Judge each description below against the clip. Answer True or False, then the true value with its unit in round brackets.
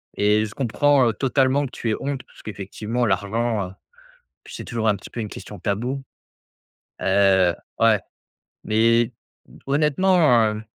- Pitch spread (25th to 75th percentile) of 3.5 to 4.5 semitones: True (4.2 semitones)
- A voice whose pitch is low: True (115 Hz)